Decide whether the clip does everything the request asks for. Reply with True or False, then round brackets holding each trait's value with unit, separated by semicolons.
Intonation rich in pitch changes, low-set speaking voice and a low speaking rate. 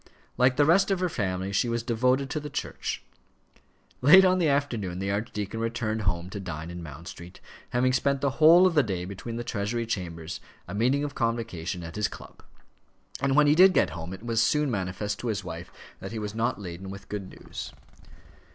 False (6.3 semitones; 115 Hz; 205 wpm)